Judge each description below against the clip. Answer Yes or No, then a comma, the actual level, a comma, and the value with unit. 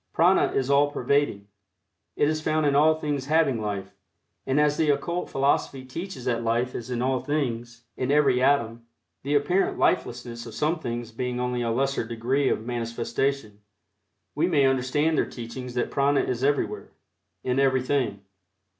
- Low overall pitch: Yes, low, 130 Hz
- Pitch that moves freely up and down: No, average, 3.3 semitones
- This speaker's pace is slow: No, average, 165 wpm